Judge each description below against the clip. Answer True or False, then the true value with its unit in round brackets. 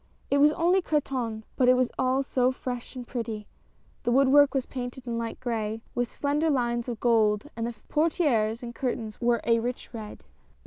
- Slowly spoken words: False (185 wpm)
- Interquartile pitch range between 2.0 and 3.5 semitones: True (2.7 semitones)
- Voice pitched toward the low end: False (245 Hz)